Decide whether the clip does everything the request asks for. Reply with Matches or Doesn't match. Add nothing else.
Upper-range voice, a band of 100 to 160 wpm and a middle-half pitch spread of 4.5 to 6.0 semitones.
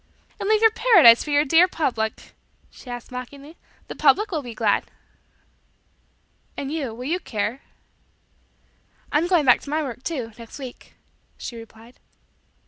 Matches